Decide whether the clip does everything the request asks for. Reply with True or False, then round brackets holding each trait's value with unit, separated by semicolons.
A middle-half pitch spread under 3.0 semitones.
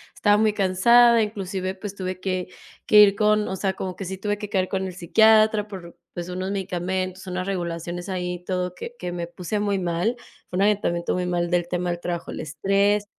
True (2.5 semitones)